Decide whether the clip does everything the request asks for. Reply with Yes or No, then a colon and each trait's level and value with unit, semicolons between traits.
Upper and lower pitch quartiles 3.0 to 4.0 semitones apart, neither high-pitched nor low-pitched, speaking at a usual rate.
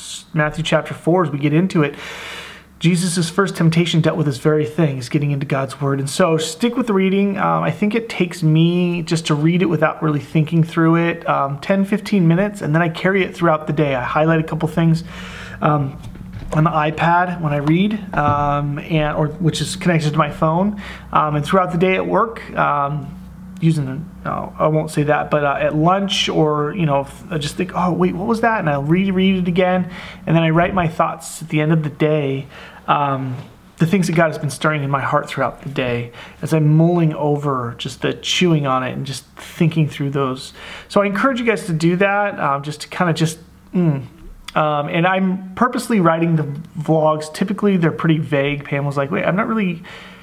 No: average, 3.4 semitones; medium, 160 Hz; fast, 220 wpm